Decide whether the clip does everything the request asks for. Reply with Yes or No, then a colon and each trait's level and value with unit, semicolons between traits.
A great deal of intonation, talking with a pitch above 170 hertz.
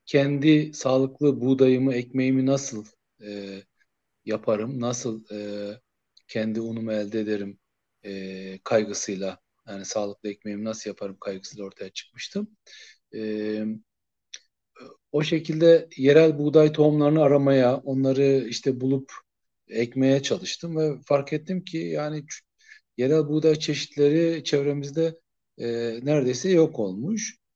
No: wide, 5.9 semitones; low, 135 Hz